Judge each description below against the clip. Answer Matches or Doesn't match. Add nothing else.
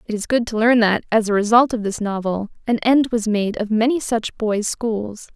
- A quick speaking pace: Matches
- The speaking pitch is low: Doesn't match